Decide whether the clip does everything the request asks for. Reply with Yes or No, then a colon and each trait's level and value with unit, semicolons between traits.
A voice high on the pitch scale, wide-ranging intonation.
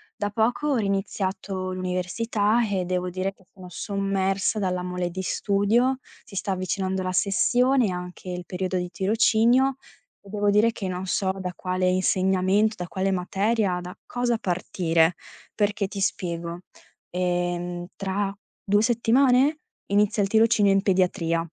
No: high, 195 Hz; narrow, 2.6 semitones